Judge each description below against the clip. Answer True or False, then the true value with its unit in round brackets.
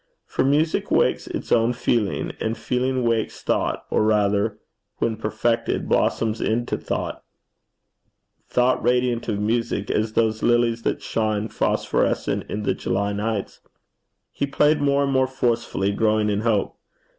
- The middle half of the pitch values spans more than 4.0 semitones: False (2.5 semitones)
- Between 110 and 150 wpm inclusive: True (140 wpm)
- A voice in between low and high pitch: False (115 Hz)